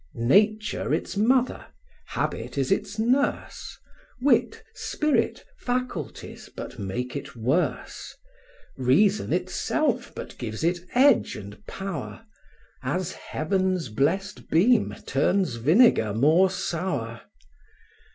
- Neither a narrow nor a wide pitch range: No, wide, 8.3 semitones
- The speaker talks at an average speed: No, slow, 100 wpm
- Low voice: No, medium, 185 Hz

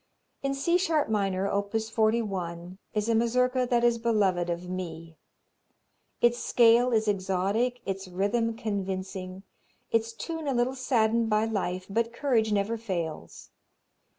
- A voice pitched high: Yes, high, 220 Hz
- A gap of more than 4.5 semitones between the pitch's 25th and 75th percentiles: No, average, 3.8 semitones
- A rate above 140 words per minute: No, slow, 135 wpm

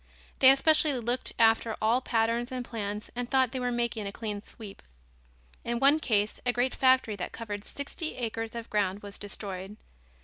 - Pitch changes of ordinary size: Yes, average, 3.3 semitones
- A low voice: No, high, 230 Hz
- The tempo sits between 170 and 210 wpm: Yes, average, 175 wpm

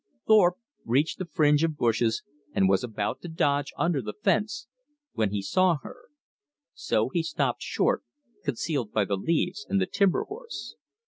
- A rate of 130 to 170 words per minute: Yes, average, 160 wpm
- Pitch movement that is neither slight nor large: No, wide, 8.4 semitones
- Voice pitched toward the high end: No, medium, 155 Hz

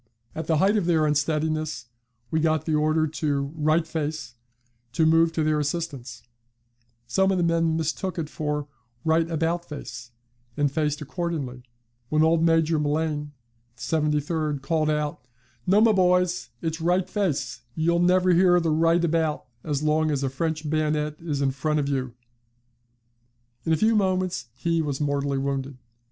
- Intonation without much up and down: Yes, narrow, 2.2 semitones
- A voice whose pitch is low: No, medium, 155 Hz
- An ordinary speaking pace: Yes, average, 160 wpm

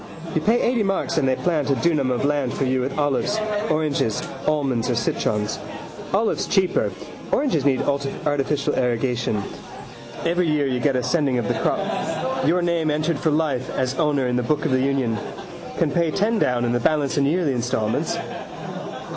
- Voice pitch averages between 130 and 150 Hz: Yes, medium, 140 Hz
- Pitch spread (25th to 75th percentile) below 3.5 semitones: No, average, 3.8 semitones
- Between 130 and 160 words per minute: No, average, 180 wpm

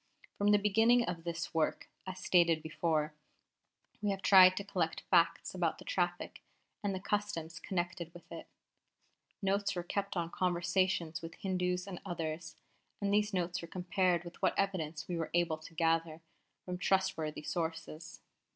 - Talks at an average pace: Yes, average, 160 wpm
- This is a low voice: No, medium, 175 Hz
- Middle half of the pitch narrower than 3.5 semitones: Yes, average, 2.7 semitones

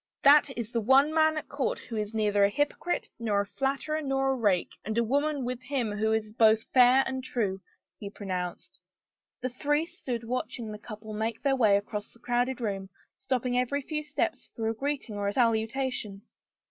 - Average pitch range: Yes, average, 4.0 semitones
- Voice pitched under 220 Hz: No, high, 240 Hz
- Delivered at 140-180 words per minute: No, average, 195 wpm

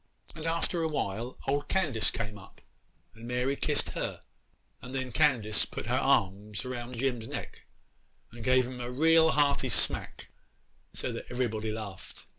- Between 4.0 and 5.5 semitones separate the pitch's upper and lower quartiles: Yes, average, 4.3 semitones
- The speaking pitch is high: No, low, 125 Hz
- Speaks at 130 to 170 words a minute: Yes, average, 155 wpm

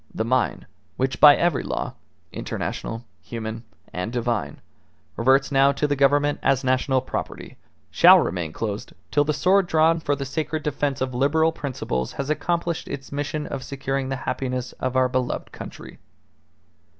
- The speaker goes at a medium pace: Yes, average, 155 wpm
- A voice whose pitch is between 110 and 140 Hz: Yes, low, 135 Hz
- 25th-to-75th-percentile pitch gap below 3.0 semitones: Yes, narrow, 2.5 semitones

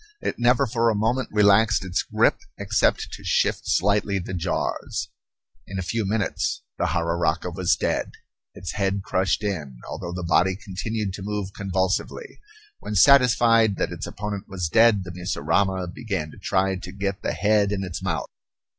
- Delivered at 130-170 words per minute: Yes, average, 165 wpm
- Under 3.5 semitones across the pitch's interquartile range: Yes, narrow, 2.5 semitones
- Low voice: Yes, low, 100 Hz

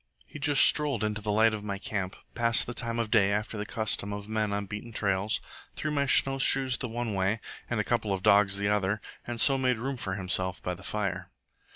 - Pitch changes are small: No, average, 3.0 semitones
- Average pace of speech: No, fast, 225 wpm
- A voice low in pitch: Yes, low, 105 Hz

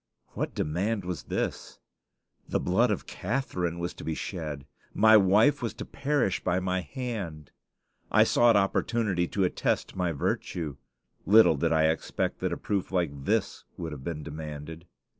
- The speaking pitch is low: Yes, very low, 90 Hz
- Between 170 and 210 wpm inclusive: No, average, 160 wpm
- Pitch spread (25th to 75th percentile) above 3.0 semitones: Yes, average, 4.8 semitones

